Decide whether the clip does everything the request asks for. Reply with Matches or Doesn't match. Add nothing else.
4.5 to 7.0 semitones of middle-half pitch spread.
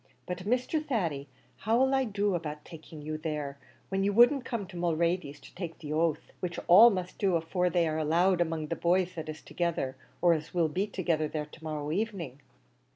Doesn't match